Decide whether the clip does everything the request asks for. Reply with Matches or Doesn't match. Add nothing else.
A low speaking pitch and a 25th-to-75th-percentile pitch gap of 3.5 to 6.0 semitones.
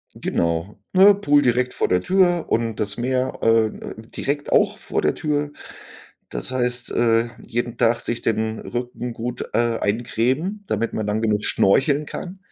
Matches